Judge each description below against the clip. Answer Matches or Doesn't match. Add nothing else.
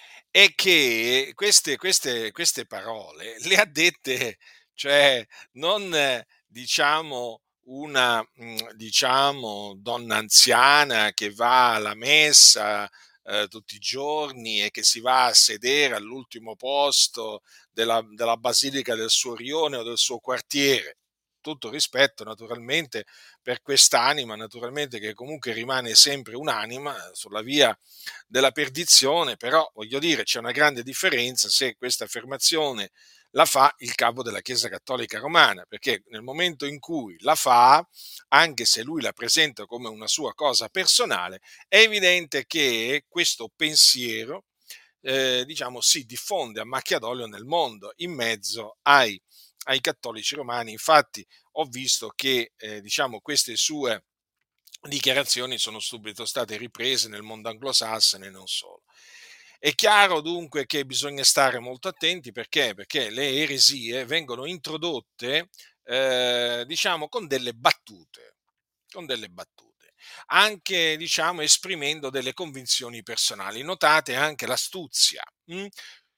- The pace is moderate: Matches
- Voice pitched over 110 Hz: Matches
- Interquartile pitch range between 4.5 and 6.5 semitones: Matches